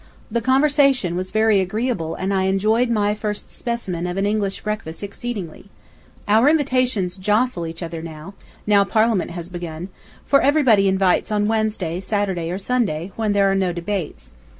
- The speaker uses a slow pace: No, average, 155 wpm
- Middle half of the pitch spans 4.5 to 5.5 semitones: No, average, 3.8 semitones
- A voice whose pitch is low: No, high, 200 Hz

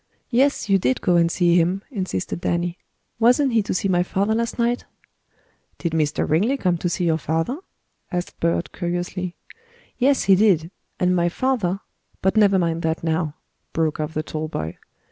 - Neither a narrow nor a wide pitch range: Yes, average, 3.8 semitones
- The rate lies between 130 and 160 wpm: No, average, 175 wpm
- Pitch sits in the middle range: Yes, medium, 175 Hz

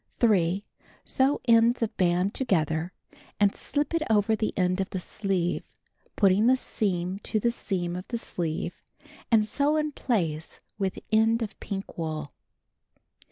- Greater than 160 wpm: No, average, 150 wpm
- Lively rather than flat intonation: No, average, 4.3 semitones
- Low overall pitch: No, high, 200 Hz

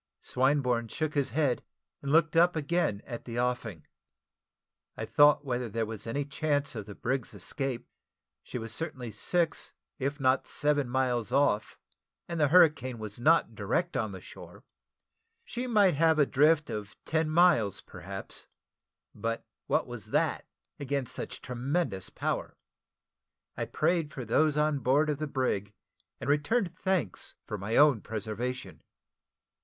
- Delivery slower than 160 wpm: Yes, average, 150 wpm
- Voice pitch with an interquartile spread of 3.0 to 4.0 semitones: No, average, 4.6 semitones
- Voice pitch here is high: No, medium, 140 Hz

